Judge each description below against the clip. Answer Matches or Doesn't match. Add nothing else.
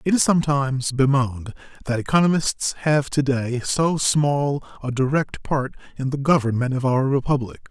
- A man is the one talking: Matches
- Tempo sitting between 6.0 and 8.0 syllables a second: Doesn't match